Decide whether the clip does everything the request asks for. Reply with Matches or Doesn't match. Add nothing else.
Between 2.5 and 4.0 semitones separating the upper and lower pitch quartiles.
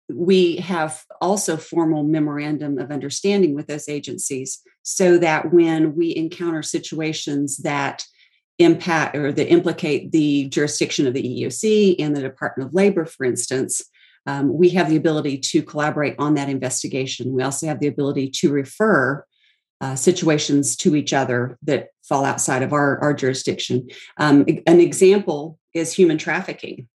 Matches